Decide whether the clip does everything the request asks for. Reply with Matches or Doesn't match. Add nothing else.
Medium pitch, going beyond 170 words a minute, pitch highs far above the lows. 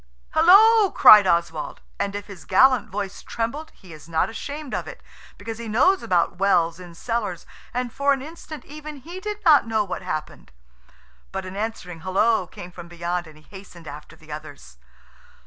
Doesn't match